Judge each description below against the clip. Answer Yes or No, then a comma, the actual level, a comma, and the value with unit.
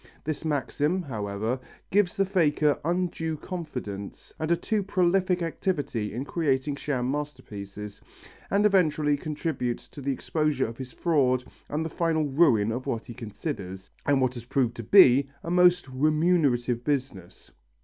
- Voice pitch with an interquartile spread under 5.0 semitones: No, average, 5.3 semitones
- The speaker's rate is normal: Yes, average, 150 wpm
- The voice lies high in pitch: No, medium, 145 Hz